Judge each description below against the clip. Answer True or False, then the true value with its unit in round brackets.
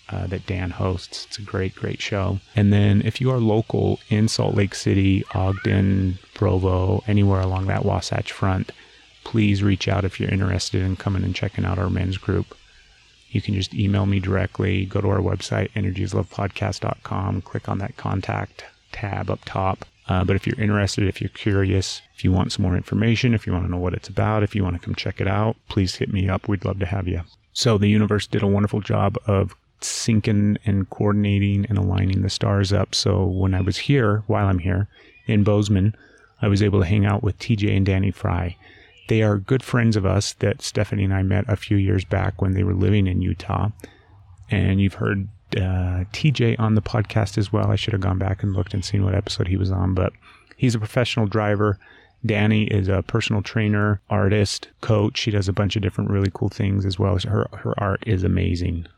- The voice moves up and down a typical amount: False (1.9 semitones)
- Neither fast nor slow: False (215 wpm)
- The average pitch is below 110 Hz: True (100 Hz)